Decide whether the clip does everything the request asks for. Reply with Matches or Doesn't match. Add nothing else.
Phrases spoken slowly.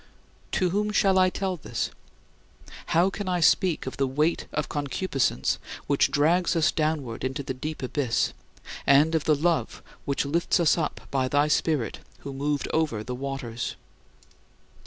Doesn't match